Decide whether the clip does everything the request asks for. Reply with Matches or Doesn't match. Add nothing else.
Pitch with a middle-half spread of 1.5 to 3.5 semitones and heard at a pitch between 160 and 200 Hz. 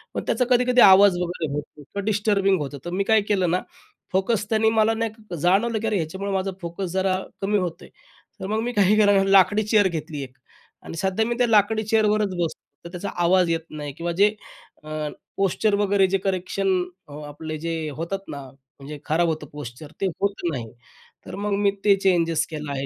Doesn't match